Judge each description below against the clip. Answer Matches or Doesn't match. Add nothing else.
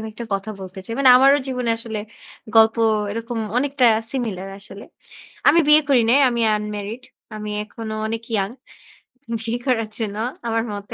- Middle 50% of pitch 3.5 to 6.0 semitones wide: Doesn't match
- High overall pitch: Matches